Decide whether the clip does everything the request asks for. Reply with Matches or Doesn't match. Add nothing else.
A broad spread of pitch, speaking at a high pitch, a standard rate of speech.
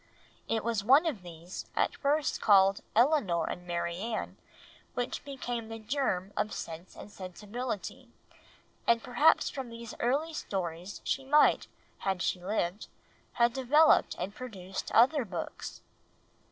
Doesn't match